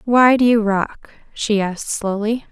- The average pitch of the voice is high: Yes, high, 220 Hz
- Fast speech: No, average, 165 wpm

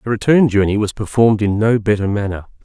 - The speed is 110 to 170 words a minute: No, fast, 205 wpm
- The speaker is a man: Yes, male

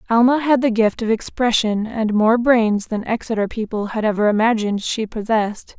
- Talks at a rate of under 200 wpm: Yes, average, 175 wpm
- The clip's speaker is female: Yes, female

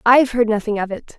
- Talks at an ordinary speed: No, fast, 250 wpm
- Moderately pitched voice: No, high, 225 Hz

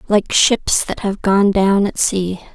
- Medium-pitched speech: No, high, 195 Hz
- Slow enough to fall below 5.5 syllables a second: Yes, 3.6 syllables/s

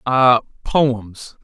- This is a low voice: Yes, low, 125 Hz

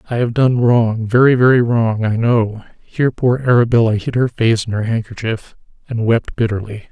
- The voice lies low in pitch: Yes, low, 115 Hz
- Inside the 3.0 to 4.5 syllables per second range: No, 5.1 syllables/s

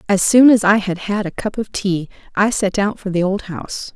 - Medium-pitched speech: No, high, 200 Hz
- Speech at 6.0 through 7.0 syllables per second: No, 5.1 syllables/s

